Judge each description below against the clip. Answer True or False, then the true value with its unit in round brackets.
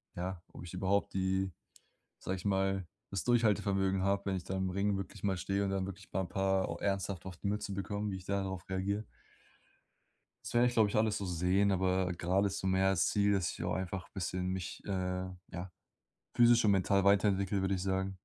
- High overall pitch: False (95 Hz)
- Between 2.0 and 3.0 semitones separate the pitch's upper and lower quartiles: False (1.1 semitones)